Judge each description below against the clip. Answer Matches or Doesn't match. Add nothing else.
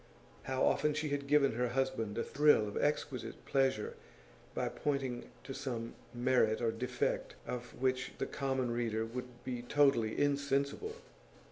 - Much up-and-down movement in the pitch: Doesn't match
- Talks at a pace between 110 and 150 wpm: Matches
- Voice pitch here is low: Matches